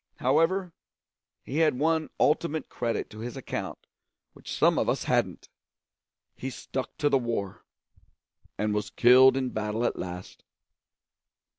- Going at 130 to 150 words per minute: Yes, slow, 135 wpm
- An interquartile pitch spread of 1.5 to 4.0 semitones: No, average, 5.2 semitones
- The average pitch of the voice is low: Yes, low, 130 Hz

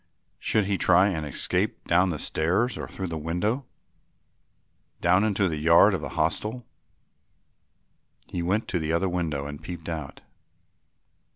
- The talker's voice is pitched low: Yes, very low, 90 Hz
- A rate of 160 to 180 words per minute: No, average, 150 wpm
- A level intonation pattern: No, average, 3.8 semitones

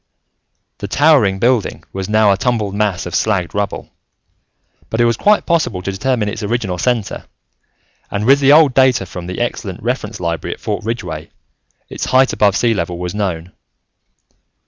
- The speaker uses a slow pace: No, average, 170 wpm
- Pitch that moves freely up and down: No, average, 4.3 semitones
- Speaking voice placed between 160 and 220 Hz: No, low, 105 Hz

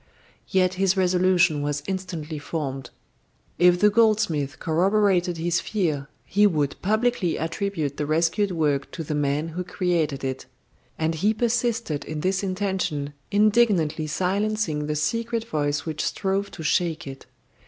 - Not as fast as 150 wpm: Yes, average, 140 wpm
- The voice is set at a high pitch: No, medium, 175 Hz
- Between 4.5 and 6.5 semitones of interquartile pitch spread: Yes, average, 4.8 semitones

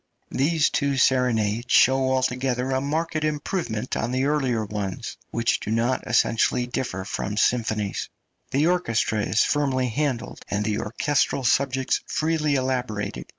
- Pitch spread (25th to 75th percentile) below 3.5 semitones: No, average, 4.0 semitones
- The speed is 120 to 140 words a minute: Yes, slow, 135 wpm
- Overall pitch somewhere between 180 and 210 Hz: No, low, 130 Hz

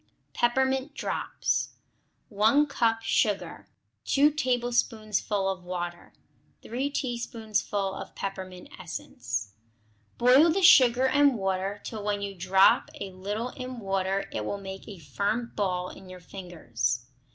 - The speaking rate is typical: No, slow, 125 wpm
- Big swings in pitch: No, average, 4.6 semitones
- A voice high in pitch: Yes, high, 205 Hz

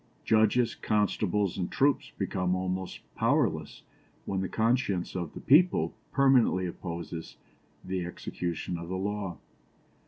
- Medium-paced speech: No, slow, 120 wpm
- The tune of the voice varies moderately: Yes, average, 3.6 semitones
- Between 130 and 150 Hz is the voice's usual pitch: No, very low, 95 Hz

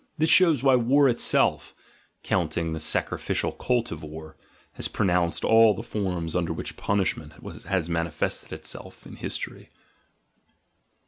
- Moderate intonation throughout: No, wide, 6.2 semitones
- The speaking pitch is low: Yes, very low, 95 Hz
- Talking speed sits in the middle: No, slow, 130 wpm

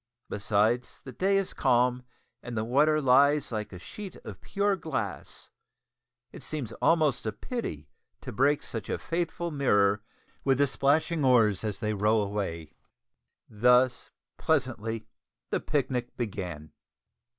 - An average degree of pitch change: No, wide, 5.7 semitones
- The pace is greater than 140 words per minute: No, slow, 135 wpm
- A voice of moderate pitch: No, low, 125 Hz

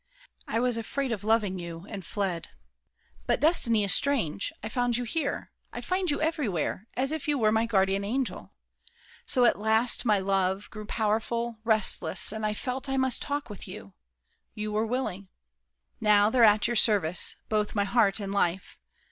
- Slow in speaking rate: No, average, 175 wpm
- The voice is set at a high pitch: Yes, high, 220 Hz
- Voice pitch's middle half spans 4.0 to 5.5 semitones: No, average, 3.6 semitones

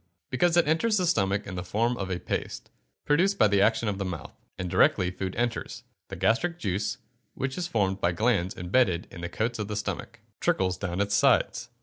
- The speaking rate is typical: No, fast, 215 wpm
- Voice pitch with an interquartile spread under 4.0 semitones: No, average, 5.0 semitones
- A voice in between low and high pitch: No, low, 105 Hz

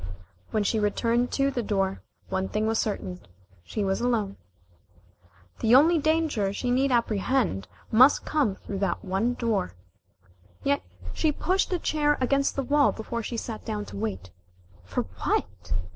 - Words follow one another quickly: No, average, 155 wpm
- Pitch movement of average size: No, wide, 5.8 semitones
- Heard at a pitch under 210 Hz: No, high, 225 Hz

